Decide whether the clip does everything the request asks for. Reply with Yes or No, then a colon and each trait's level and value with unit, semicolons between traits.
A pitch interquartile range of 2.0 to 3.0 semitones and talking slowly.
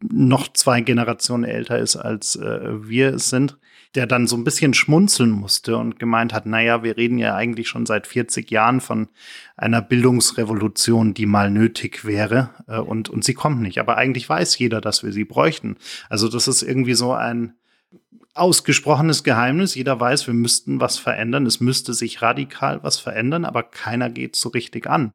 No: narrow, 2.6 semitones; average, 185 wpm